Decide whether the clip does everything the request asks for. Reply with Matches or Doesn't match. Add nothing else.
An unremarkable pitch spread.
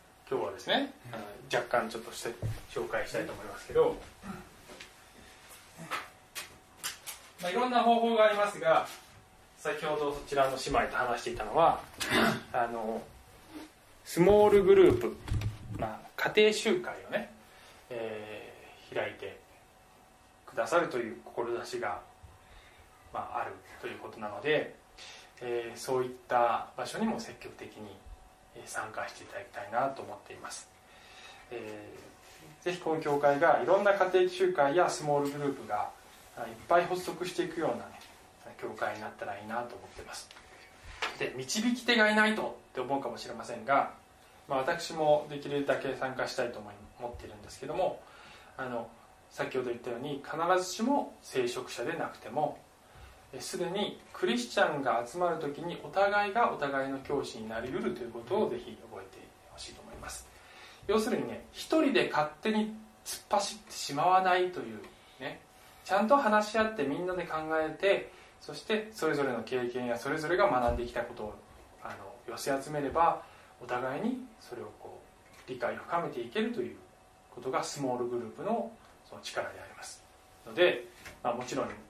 Doesn't match